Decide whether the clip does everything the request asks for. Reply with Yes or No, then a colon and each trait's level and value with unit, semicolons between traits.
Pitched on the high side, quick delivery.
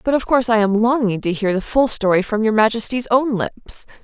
Yes: high, 225 Hz; fast, 240 wpm